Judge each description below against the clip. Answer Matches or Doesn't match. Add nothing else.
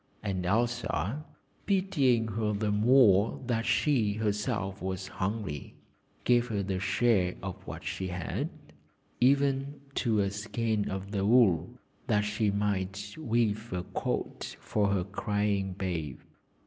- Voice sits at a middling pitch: Doesn't match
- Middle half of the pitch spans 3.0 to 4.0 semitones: Matches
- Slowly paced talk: Matches